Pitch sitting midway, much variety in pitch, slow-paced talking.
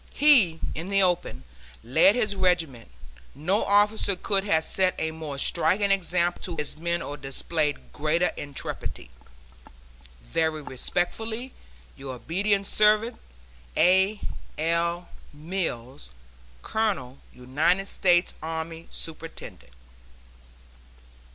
No: medium, 170 Hz; average, 4.3 semitones; slow, 100 wpm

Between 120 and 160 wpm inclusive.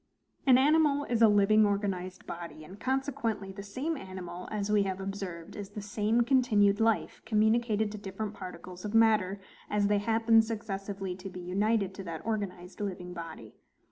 No: average, 170 wpm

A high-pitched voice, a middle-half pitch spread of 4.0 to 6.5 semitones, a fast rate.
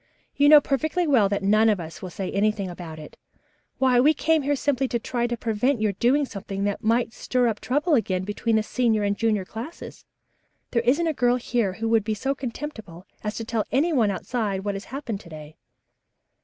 Yes: high, 225 Hz; average, 4.5 semitones; fast, 220 wpm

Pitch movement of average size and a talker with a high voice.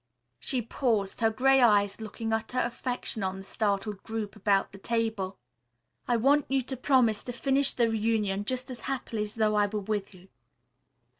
Yes: average, 3.3 semitones; high, 220 Hz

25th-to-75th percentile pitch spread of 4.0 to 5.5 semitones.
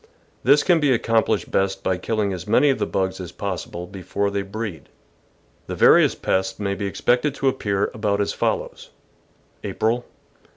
No: average, 3.2 semitones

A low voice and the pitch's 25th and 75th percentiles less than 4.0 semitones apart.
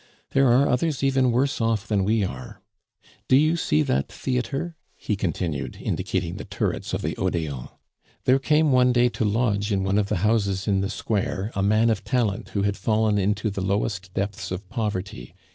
No: low, 105 Hz; average, 4.4 semitones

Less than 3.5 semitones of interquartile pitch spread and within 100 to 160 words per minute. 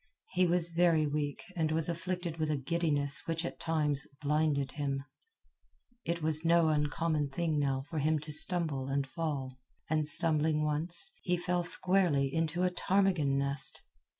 Yes: average, 2.8 semitones; average, 155 wpm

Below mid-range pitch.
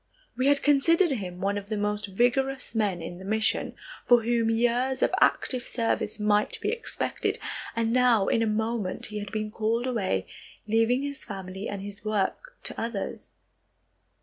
No: high, 225 Hz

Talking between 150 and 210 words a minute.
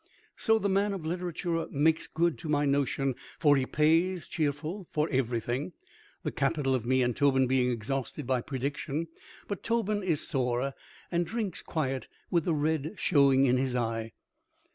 Yes: average, 165 wpm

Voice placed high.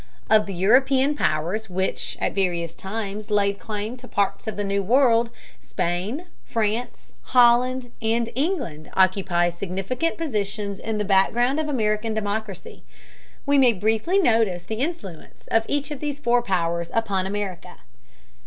Yes: high, 215 Hz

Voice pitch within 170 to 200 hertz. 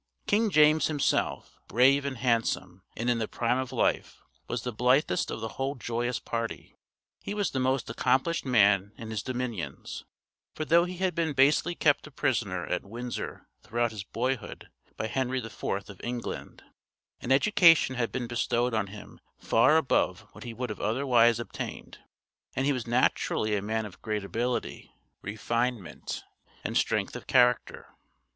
No: low, 120 Hz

